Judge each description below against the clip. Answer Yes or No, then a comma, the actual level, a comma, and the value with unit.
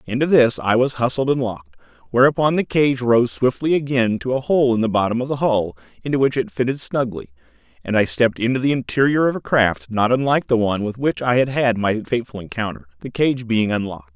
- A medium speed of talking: No, fast, 220 wpm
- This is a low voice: Yes, low, 120 Hz